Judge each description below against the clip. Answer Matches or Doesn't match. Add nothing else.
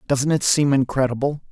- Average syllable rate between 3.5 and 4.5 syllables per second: Doesn't match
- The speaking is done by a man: Matches